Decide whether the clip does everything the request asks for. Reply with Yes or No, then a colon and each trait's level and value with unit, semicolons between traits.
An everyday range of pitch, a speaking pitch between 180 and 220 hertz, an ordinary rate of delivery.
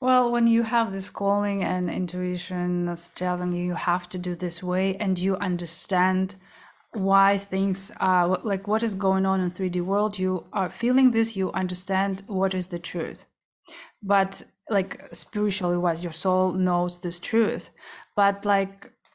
No: narrow, 1.9 semitones; high, 190 Hz; average, 165 wpm